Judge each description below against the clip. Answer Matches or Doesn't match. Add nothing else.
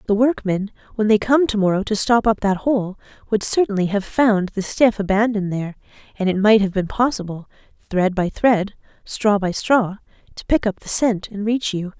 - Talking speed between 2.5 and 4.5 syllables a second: Doesn't match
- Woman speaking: Matches